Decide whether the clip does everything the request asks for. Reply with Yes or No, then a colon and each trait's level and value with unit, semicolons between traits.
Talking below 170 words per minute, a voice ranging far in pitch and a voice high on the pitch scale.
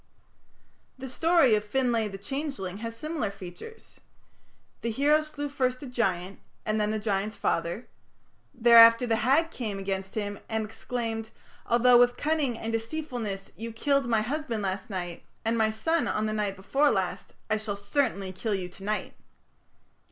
No: average, 160 wpm; average, 4.1 semitones; high, 225 Hz